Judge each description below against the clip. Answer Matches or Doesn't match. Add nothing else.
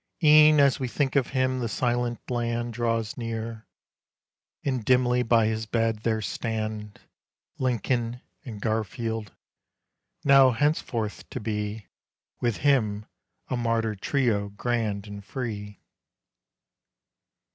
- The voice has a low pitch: Matches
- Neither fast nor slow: Doesn't match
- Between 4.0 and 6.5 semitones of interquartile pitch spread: Doesn't match